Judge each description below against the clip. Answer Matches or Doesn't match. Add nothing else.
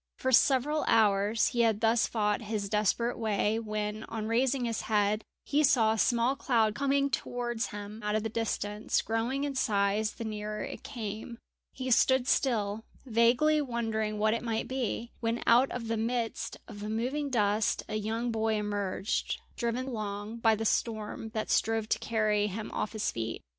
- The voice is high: Matches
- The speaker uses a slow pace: Doesn't match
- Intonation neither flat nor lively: Doesn't match